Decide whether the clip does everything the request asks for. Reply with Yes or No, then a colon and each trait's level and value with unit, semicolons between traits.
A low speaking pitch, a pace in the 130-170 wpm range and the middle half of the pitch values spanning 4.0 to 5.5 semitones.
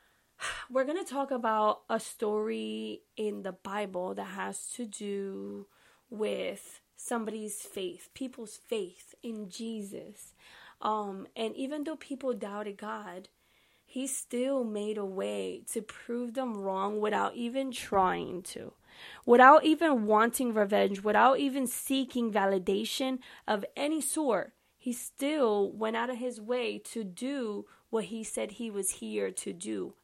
No: high, 225 Hz; average, 140 wpm; average, 4.3 semitones